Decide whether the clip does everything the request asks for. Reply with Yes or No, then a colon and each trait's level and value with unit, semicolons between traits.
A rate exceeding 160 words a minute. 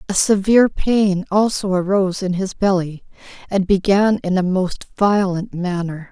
No: average, 145 wpm